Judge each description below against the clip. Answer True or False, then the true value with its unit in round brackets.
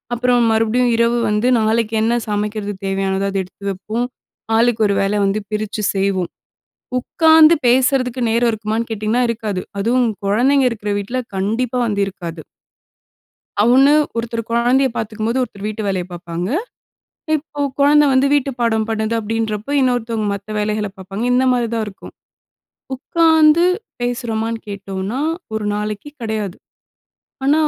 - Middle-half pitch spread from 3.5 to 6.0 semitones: False (3.1 semitones)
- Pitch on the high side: True (225 Hz)